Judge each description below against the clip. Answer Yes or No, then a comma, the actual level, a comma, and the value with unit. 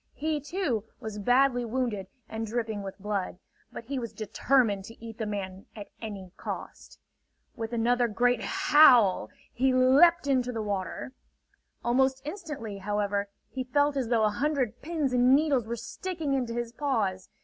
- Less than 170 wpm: Yes, average, 160 wpm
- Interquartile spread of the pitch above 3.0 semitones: Yes, average, 4.2 semitones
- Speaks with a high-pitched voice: Yes, high, 240 Hz